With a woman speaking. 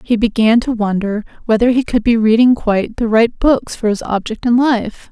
Yes: female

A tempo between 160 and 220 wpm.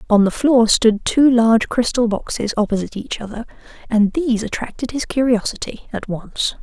Yes: average, 165 wpm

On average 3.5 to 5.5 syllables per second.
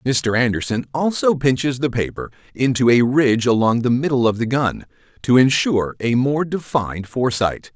Yes: 5.2 syllables/s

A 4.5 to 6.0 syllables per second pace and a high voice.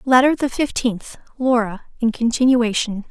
Yes: 4.6 syllables/s; high, 240 Hz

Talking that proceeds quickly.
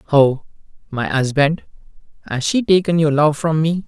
No: average, 155 wpm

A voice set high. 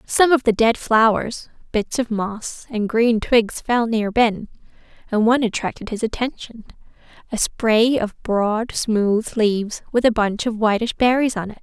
Yes: high, 225 Hz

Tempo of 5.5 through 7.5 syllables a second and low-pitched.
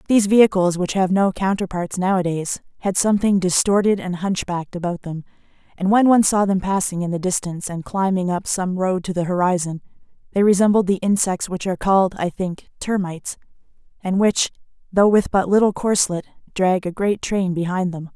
No: 5.6 syllables/s; high, 190 Hz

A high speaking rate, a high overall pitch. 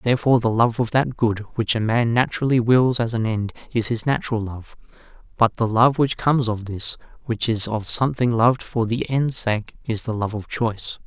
No: fast, 210 wpm; low, 115 Hz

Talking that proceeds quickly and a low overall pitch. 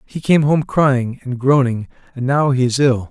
Yes: fast, 210 wpm; low, 130 Hz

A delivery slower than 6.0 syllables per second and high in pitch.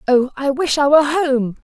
Yes: 5.0 syllables/s; very high, 280 Hz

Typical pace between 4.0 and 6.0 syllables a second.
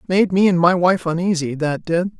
Yes: 5.1 syllables/s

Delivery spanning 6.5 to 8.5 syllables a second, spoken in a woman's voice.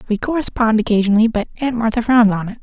Yes: 6.8 syllables/s; female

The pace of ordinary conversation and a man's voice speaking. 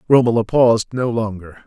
Yes: average, 145 wpm; male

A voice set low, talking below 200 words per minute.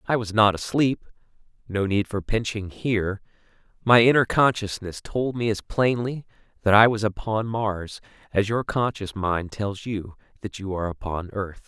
Yes: low, 105 Hz; average, 165 wpm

